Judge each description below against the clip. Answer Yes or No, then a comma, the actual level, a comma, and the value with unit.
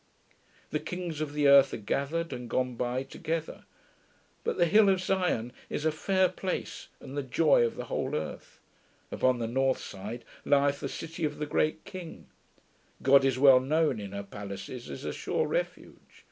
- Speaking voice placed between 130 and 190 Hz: Yes, medium, 140 Hz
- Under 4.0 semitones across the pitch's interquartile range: No, average, 4.7 semitones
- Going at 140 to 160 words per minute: No, average, 180 wpm